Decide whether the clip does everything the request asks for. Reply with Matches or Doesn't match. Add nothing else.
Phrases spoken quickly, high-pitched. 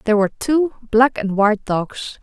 Doesn't match